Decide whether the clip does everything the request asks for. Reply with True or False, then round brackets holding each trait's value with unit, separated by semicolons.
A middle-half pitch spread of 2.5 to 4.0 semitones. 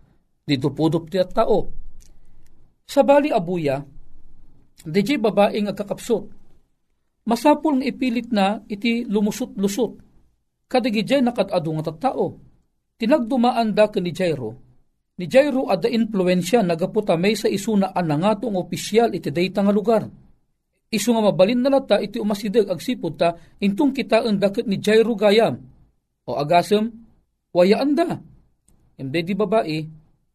False (4.9 semitones)